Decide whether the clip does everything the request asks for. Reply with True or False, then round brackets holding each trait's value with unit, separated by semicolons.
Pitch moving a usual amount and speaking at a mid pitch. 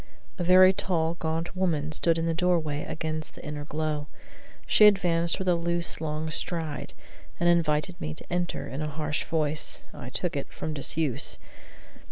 False (2.2 semitones; 160 Hz)